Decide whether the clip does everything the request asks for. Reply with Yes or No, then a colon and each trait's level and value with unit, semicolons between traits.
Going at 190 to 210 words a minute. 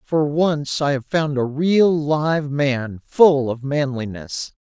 No: average, 155 wpm